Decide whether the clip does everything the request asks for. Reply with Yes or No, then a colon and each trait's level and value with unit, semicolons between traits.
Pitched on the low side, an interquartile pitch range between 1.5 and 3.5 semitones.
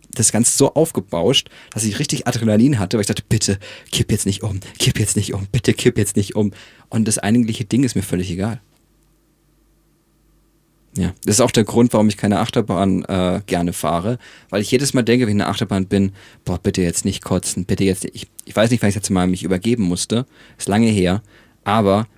No: low, 110 Hz; average, 4.1 semitones